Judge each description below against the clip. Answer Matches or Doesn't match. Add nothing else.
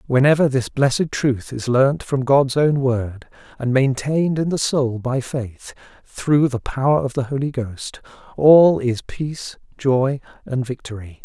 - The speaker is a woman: Doesn't match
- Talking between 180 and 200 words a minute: Doesn't match